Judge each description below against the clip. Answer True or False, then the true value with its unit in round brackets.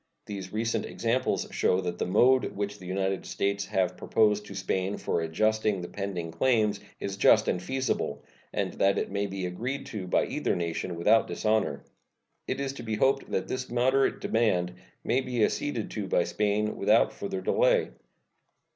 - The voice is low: True (105 Hz)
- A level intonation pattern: False (3.4 semitones)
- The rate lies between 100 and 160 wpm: False (175 wpm)